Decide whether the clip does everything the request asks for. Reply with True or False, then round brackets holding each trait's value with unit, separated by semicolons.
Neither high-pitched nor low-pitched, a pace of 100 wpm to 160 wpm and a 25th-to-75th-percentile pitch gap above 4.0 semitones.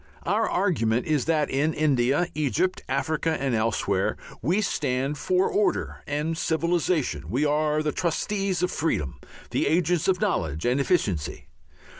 True (155 Hz; 140 wpm; 5.1 semitones)